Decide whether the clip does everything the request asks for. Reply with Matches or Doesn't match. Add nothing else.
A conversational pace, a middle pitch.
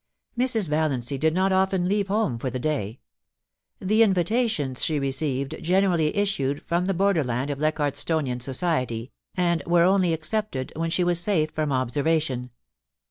Matches